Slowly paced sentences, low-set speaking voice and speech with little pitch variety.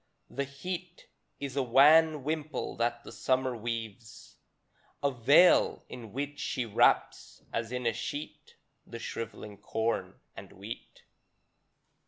No: slow, 125 wpm; low, 125 Hz; average, 3.8 semitones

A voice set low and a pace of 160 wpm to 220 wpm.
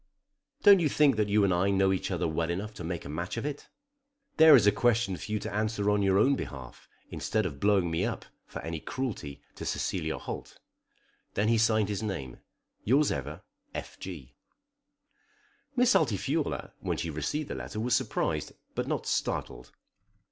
Yes: low, 100 Hz; average, 185 wpm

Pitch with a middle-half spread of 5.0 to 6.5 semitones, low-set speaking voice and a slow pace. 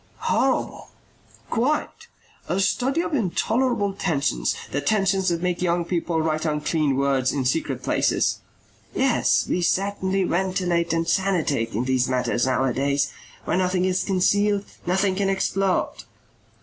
No: wide, 5.5 semitones; medium, 175 Hz; slow, 130 wpm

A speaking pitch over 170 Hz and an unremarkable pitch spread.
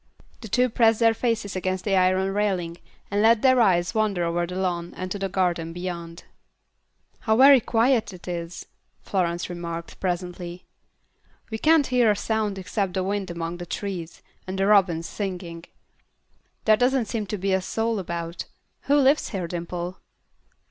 Yes: high, 190 Hz; average, 3.9 semitones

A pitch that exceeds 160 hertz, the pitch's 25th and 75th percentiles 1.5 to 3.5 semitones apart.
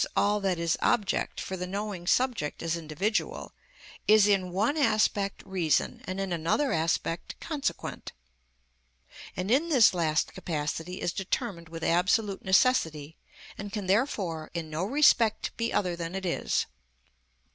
No: high, 190 Hz; average, 4.3 semitones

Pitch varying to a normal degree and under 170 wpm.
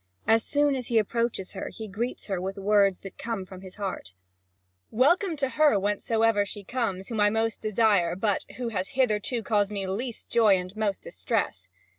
No: average, 3.1 semitones; average, 190 wpm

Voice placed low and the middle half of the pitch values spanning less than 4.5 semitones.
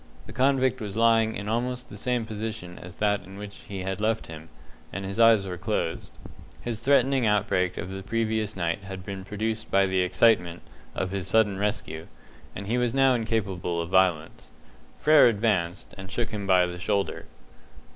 Yes: low, 105 Hz; average, 3.3 semitones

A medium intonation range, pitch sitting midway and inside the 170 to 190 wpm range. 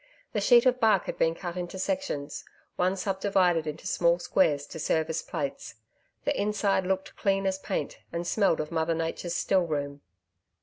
Yes: average, 3.3 semitones; medium, 180 Hz; average, 180 wpm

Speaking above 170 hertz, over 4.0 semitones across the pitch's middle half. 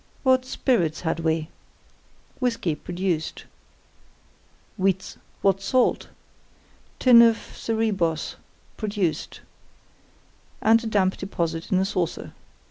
Yes: high, 190 Hz; average, 5.1 semitones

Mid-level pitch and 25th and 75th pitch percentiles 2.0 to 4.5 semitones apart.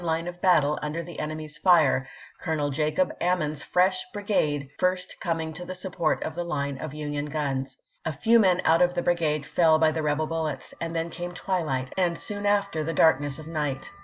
Yes: medium, 160 Hz; average, 2.9 semitones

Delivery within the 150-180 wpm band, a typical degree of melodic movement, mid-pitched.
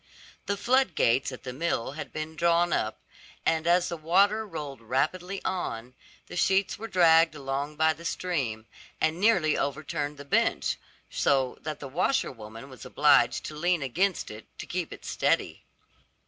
Yes: average, 160 wpm; average, 4.6 semitones; medium, 155 Hz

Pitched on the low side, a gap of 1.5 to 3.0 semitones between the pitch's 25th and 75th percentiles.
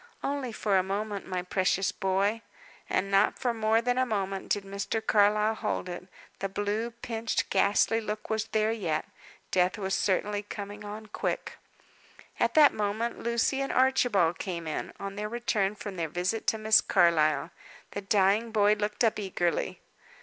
No: high, 205 Hz; narrow, 2.5 semitones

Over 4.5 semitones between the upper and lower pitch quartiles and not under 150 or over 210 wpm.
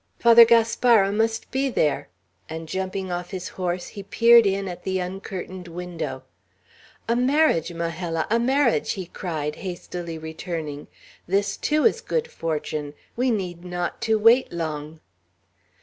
No: average, 5.2 semitones; average, 140 wpm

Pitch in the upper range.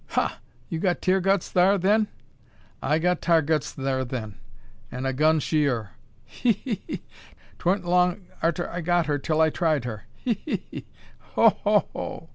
No: medium, 165 Hz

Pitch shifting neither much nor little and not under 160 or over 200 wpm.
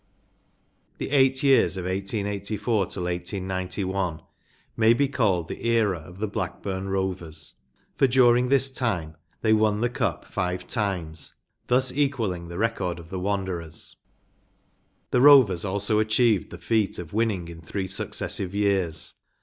No: average, 4.2 semitones; average, 145 wpm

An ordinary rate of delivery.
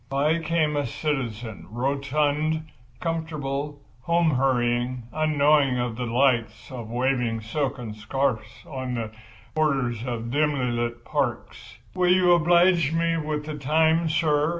No: slow, 125 wpm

